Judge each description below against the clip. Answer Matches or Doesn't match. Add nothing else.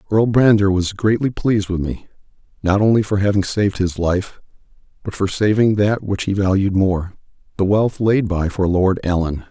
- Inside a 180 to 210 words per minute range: Matches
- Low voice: Matches